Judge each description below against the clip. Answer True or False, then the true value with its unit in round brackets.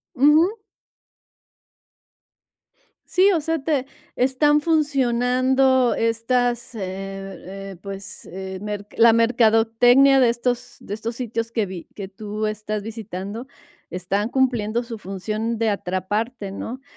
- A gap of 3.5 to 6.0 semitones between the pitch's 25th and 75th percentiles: True (3.9 semitones)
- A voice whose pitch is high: True (230 Hz)